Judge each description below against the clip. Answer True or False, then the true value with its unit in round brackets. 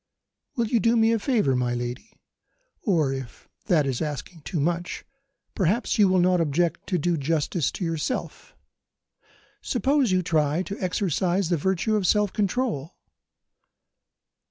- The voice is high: False (175 Hz)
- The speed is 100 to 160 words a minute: True (145 wpm)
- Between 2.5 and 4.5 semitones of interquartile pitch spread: False (5.4 semitones)